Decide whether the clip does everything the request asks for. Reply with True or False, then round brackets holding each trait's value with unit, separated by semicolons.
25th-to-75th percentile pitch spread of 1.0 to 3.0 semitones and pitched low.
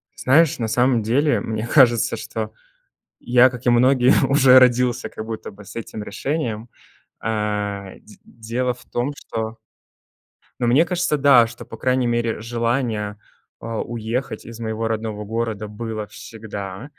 True (2.5 semitones; 115 Hz)